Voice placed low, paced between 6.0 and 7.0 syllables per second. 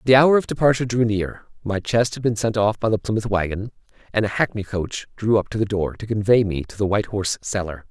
Yes: low, 105 Hz; 6.1 syllables/s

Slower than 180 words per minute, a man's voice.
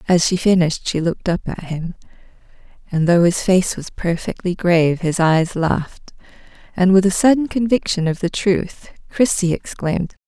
No: average, 165 wpm; female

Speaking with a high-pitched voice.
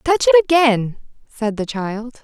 Yes: very high, 255 Hz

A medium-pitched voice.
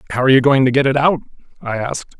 No: low, 130 Hz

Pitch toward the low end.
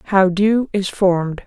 No: high, 190 Hz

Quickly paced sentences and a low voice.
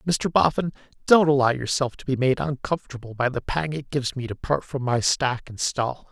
Yes: fast, 215 wpm; low, 130 Hz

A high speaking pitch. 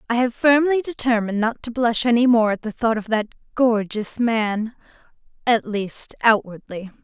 Yes: high, 230 Hz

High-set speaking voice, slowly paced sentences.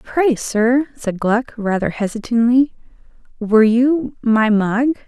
Yes: high, 235 Hz; slow, 120 wpm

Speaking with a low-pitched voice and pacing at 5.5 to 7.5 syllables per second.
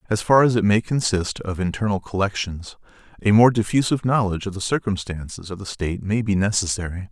Yes: low, 100 Hz; 6.1 syllables/s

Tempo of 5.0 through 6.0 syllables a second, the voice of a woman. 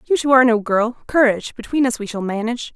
No: 6.8 syllables/s; female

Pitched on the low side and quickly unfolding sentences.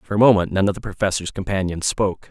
Yes: very low, 95 Hz; fast, 235 wpm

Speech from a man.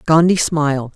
No: female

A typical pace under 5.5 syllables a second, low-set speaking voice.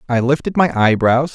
Yes: 5.1 syllables/s; low, 130 Hz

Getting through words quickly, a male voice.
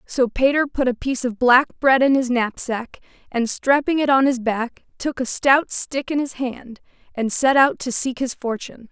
No: fast, 210 wpm; female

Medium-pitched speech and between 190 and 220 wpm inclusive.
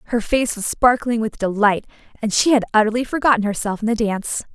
No: high, 225 Hz; average, 200 wpm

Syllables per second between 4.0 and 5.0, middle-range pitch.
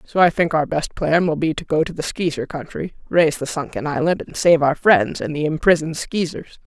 No: 5.6 syllables/s; medium, 160 Hz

